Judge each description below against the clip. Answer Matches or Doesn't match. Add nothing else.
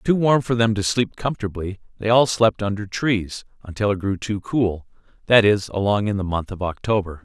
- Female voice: Doesn't match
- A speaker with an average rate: Doesn't match